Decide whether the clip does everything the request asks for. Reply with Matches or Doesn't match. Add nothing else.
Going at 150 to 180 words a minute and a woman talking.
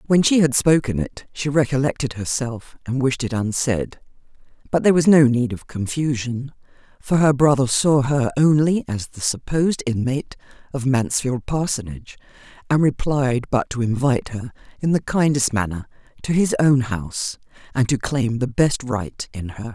Matches